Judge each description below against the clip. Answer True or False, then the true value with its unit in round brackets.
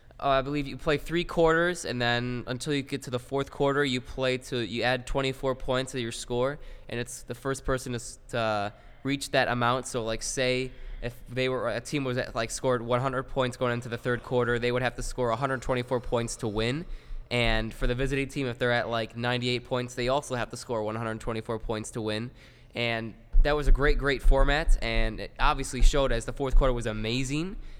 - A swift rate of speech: True (215 wpm)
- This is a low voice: True (125 Hz)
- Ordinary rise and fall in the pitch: False (2.1 semitones)